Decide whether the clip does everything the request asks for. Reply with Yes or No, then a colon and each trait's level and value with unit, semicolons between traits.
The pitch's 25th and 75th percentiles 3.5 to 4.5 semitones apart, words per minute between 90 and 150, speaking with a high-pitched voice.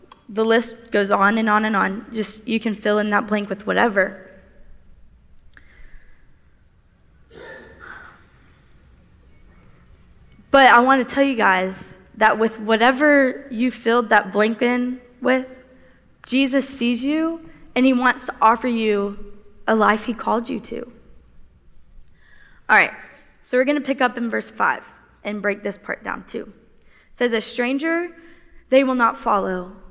Yes: average, 3.9 semitones; average, 145 wpm; high, 225 Hz